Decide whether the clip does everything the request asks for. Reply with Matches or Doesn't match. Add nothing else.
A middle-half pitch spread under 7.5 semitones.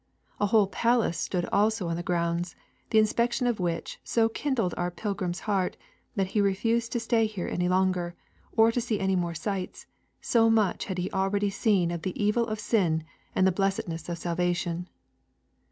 Matches